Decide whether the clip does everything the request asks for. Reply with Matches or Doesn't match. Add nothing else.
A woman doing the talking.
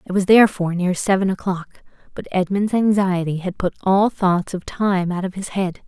Matches